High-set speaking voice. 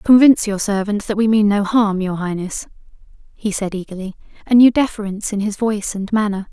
Yes: high, 205 Hz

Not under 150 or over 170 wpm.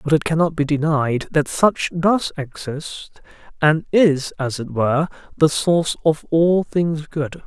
Yes: average, 160 wpm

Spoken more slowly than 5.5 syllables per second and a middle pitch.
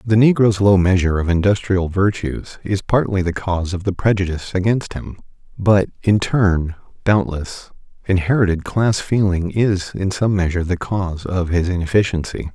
No: 5.0 syllables/s; very low, 95 Hz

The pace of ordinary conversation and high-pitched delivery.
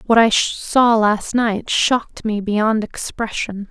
Yes: average, 145 wpm; high, 220 Hz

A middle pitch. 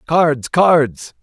Yes: medium, 155 Hz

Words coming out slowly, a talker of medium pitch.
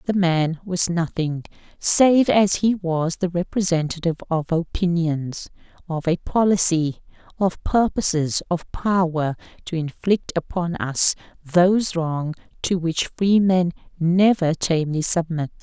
Yes: slow, 120 wpm; medium, 175 Hz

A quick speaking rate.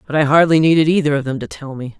Yes: fast, 300 wpm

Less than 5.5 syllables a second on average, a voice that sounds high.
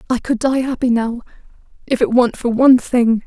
No: 5.8 syllables/s; high, 245 Hz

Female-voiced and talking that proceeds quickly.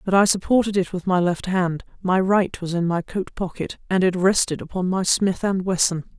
Yes: female; fast, 215 wpm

